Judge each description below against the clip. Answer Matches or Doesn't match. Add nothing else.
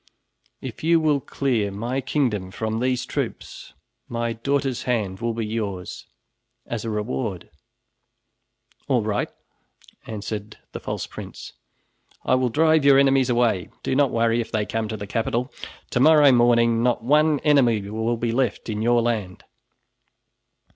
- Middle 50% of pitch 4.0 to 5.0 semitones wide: Doesn't match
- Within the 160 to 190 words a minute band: Doesn't match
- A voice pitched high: Doesn't match